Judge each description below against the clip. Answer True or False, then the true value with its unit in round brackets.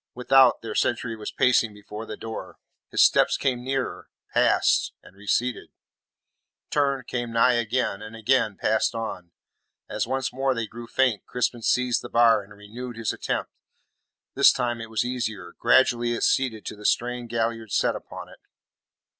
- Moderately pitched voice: False (115 Hz)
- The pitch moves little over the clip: True (2.3 semitones)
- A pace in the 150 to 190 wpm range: True (165 wpm)